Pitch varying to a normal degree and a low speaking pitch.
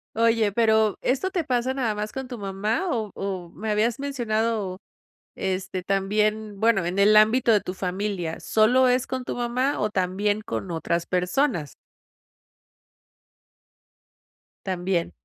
No: average, 3.8 semitones; high, 215 Hz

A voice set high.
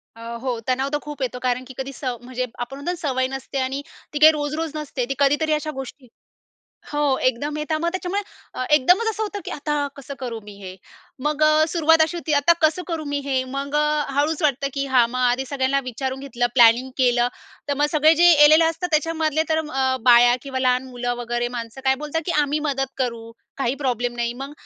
Yes: very high, 275 Hz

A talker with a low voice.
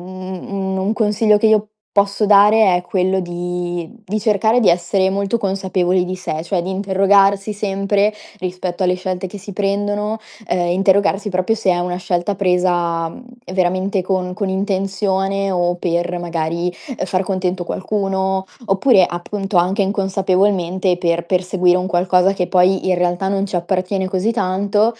No: high, 190 Hz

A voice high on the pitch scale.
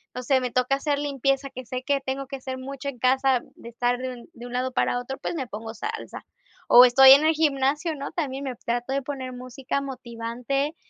Yes: very high, 265 Hz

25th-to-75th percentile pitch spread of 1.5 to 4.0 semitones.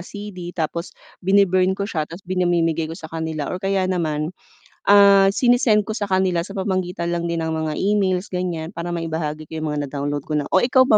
Yes: average, 3.3 semitones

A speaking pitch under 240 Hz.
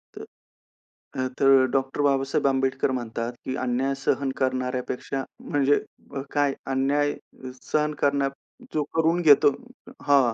Yes: low, 135 Hz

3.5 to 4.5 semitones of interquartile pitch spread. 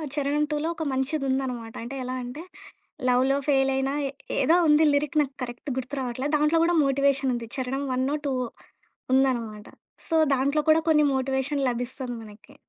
No: narrow, 2.6 semitones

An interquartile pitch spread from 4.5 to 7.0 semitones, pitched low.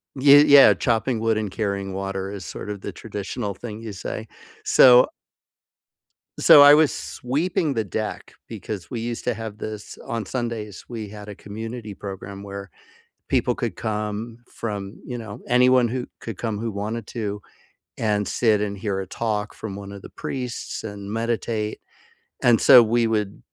No: average, 2.7 semitones; low, 110 Hz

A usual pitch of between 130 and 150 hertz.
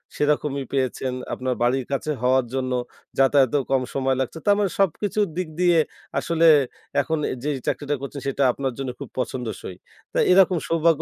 Yes: medium, 140 Hz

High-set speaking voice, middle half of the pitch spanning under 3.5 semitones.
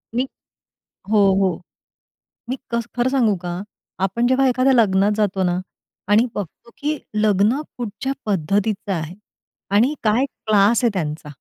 No: high, 215 Hz; average, 3.9 semitones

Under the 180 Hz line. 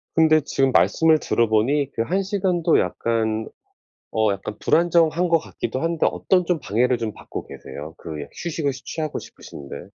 Yes: medium, 140 Hz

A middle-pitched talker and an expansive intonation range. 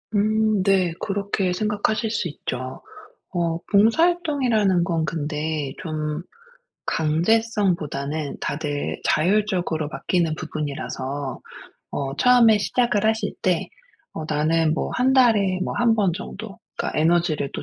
Yes: medium, 180 Hz; wide, 5.8 semitones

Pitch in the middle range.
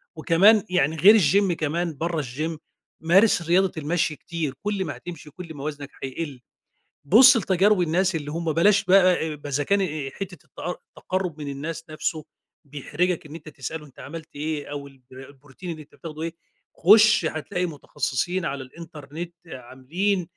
Yes: medium, 160 Hz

